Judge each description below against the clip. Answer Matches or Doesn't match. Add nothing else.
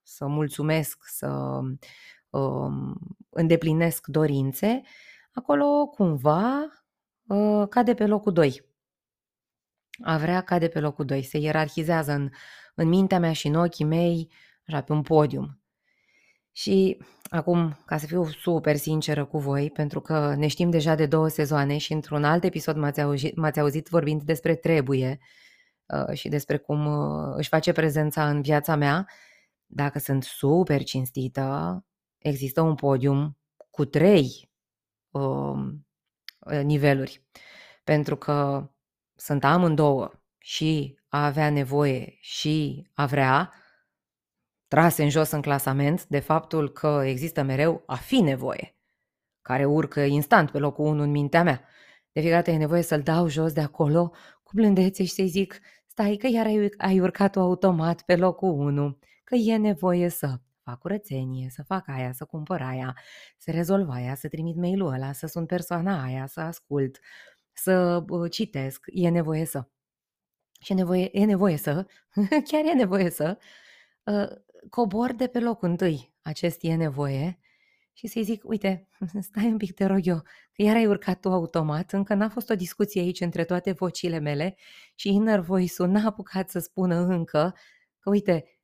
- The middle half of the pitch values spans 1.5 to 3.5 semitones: Doesn't match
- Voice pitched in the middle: Matches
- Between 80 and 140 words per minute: Doesn't match